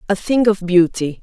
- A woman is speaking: Yes, female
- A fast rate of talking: No, average, 195 wpm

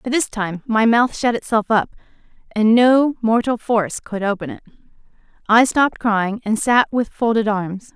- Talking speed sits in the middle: Yes, average, 165 wpm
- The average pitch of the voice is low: No, high, 225 Hz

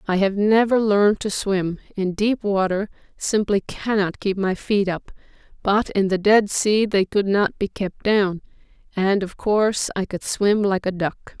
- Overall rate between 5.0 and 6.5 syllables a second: No, 4.4 syllables/s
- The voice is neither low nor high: No, high, 200 Hz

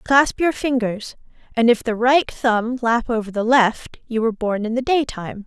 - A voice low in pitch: No, high, 235 Hz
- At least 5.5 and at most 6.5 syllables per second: No, 4.7 syllables/s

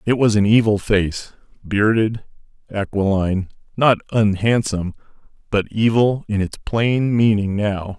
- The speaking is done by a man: Yes, male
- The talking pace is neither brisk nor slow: No, slow, 120 wpm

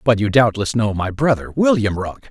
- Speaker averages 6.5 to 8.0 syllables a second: No, 5.1 syllables/s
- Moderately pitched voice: No, low, 115 Hz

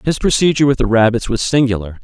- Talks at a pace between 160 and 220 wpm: Yes, fast, 205 wpm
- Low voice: Yes, low, 125 Hz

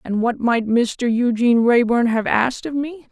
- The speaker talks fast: No, average, 195 wpm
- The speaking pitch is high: Yes, high, 240 Hz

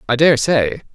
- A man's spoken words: Yes, male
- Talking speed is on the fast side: No, average, 190 wpm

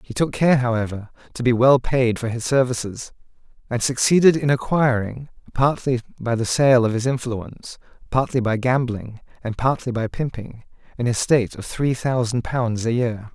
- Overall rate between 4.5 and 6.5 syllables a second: Yes, 4.9 syllables/s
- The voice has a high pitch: No, low, 125 Hz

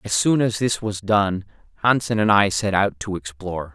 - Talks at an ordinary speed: No, fast, 210 wpm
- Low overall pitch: Yes, low, 100 Hz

